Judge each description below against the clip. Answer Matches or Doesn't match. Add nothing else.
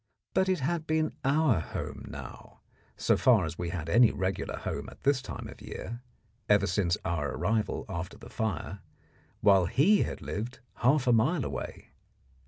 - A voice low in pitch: Matches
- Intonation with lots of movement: Matches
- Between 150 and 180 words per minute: Matches